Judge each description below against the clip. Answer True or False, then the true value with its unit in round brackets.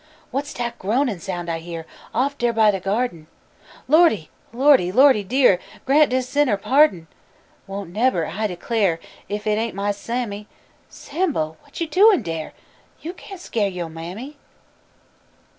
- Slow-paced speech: False (150 wpm)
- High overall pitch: True (220 Hz)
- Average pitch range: False (6.8 semitones)